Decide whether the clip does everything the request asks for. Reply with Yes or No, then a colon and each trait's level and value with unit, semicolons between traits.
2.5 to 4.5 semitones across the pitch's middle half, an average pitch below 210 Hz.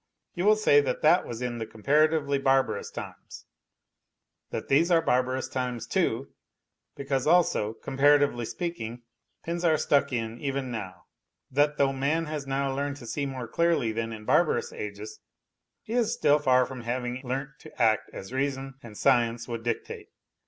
Yes: average, 3.5 semitones; low, 135 Hz